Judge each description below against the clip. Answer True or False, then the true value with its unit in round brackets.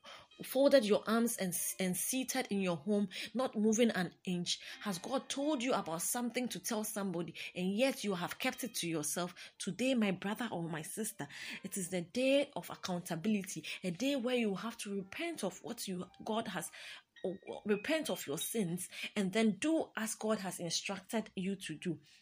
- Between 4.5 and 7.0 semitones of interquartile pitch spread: True (5.0 semitones)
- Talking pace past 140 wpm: True (185 wpm)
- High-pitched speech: True (205 Hz)